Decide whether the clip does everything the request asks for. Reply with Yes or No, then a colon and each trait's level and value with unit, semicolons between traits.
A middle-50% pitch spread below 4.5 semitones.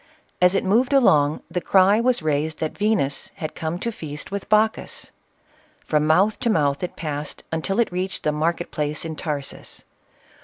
No: average, 5.0 semitones